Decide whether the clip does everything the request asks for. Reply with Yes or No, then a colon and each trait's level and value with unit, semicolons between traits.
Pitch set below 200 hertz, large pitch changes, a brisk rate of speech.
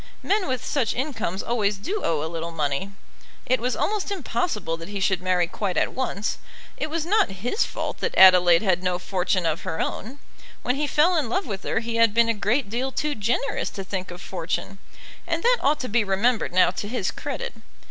No: high, 215 Hz; wide, 6.5 semitones; fast, 210 wpm